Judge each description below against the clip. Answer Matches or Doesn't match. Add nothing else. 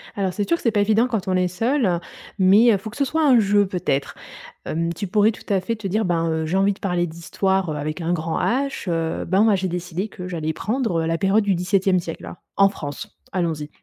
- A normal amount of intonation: Matches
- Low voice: Doesn't match